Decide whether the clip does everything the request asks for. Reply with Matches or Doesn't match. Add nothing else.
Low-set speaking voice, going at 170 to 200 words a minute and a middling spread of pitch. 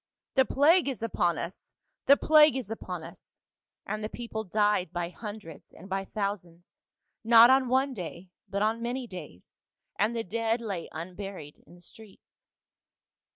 Doesn't match